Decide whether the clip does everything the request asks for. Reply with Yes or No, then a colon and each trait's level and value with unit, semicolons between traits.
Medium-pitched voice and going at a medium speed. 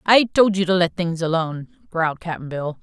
No: medium, 175 Hz; fast, 210 wpm